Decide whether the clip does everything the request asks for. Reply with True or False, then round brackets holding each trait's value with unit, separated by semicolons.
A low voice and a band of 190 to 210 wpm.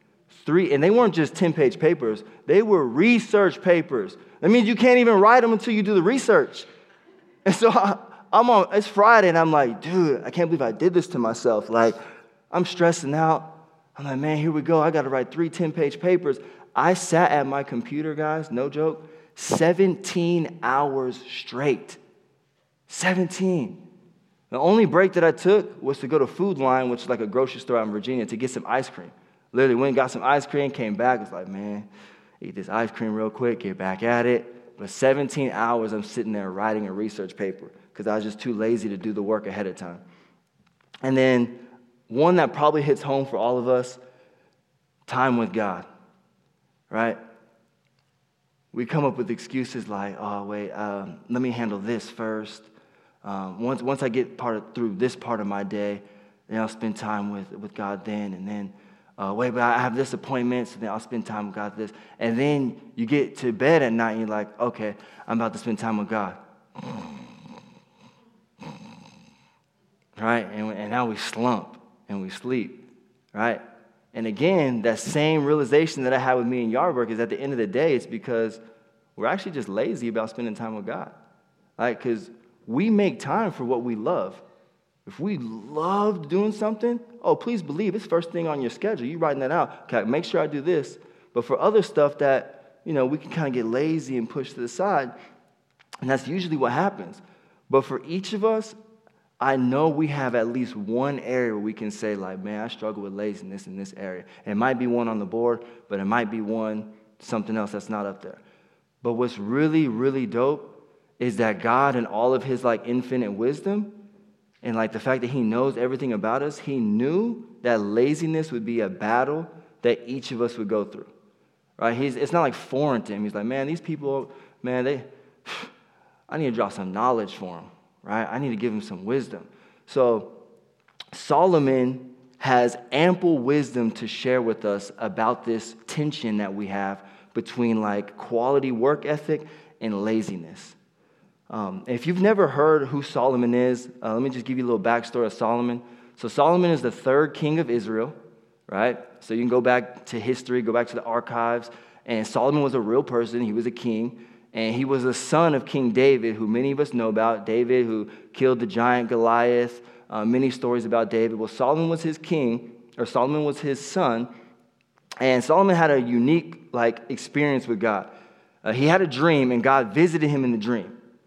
True (125 Hz; 200 wpm)